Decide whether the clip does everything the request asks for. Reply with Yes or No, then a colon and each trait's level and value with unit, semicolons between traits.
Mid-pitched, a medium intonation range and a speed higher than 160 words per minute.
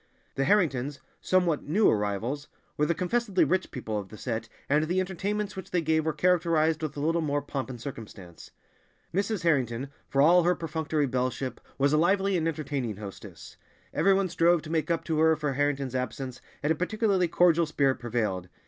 Yes: medium, 155 Hz; average, 4.9 semitones; average, 175 wpm